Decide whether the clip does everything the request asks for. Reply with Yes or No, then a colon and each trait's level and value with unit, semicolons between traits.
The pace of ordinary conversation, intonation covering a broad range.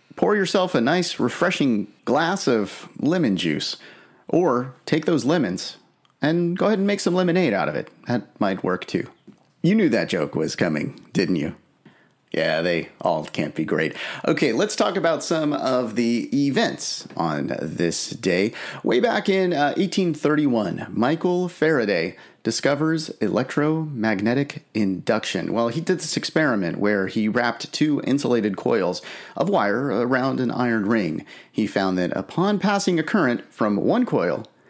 Yes: average, 155 wpm; wide, 7.2 semitones